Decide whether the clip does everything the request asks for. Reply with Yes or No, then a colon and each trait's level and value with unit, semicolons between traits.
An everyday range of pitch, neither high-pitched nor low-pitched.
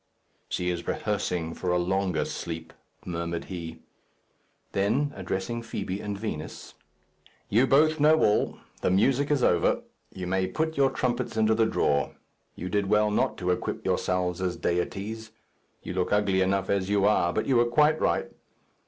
No: average, 4.1 semitones; low, 100 Hz